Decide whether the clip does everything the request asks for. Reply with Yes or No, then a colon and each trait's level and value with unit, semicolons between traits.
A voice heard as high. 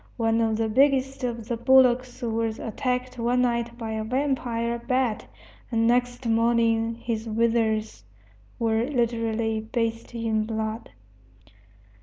Yes: high, 230 Hz